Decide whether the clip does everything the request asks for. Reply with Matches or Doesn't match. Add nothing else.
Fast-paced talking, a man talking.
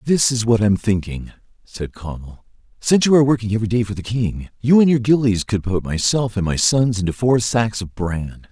Matches